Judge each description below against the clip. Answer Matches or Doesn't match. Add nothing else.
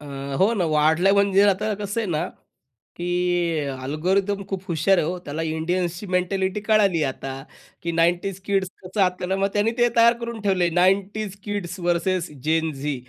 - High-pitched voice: Doesn't match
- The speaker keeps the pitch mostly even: Doesn't match